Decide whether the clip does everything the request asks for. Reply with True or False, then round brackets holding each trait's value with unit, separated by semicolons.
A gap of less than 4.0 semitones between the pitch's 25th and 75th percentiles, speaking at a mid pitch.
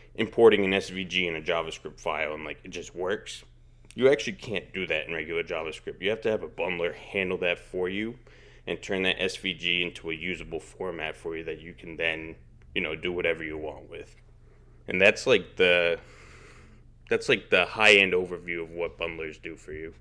False (3.5 semitones; 90 Hz)